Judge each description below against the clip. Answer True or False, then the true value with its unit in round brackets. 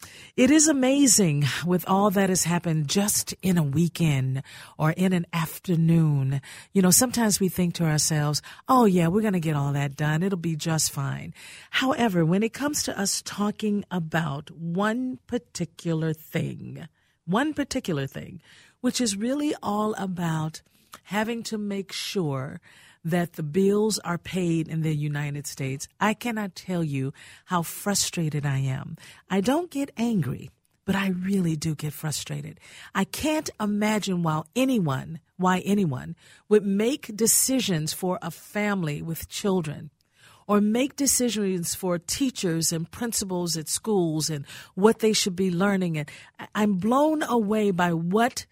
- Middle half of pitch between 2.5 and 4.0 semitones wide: False (5.0 semitones)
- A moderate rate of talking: True (150 wpm)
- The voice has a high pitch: False (180 Hz)